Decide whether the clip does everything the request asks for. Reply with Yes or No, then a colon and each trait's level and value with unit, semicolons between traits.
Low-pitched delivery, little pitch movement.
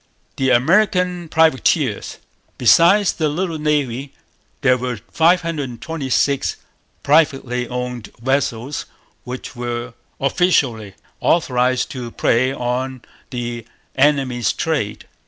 No: low, 130 Hz; average, 4.4 semitones